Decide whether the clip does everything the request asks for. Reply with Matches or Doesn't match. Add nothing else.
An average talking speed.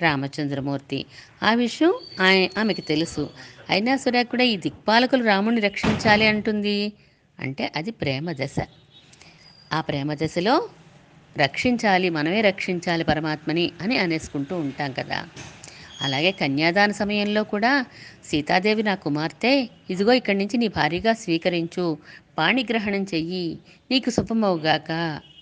Matches